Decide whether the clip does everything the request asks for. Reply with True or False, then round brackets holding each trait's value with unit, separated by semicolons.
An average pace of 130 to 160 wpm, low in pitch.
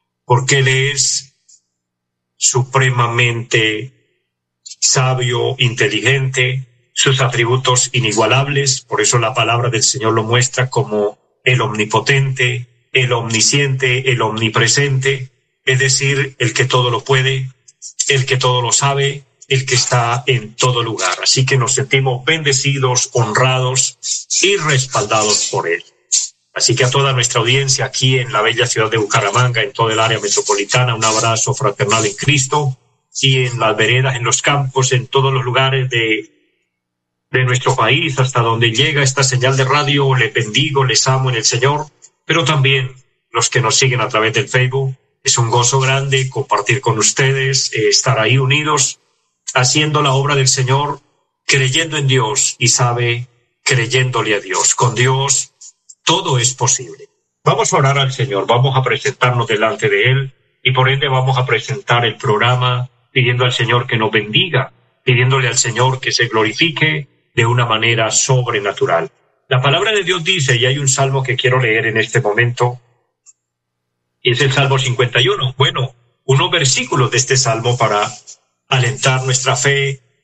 True (155 wpm; 130 Hz)